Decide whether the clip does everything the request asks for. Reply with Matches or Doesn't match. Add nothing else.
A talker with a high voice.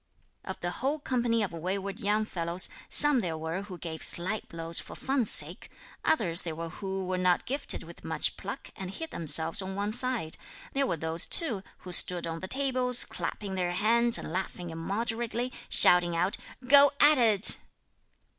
Matches